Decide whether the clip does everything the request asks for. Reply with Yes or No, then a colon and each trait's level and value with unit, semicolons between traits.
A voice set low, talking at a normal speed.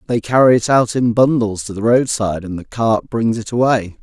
No: low, 115 Hz; fast, 225 wpm